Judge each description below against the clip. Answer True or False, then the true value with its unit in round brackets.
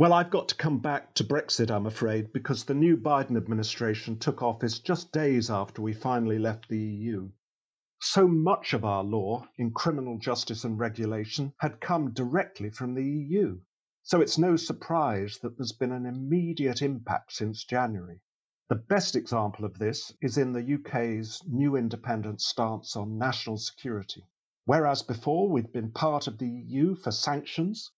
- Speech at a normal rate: True (165 wpm)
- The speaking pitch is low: True (125 Hz)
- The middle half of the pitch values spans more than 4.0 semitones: True (4.8 semitones)